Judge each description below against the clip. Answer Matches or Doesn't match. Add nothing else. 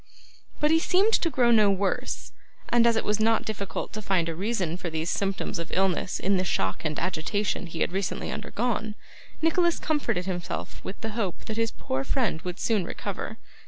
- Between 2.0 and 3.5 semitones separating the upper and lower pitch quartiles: Doesn't match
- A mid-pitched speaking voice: Doesn't match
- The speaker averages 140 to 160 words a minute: Doesn't match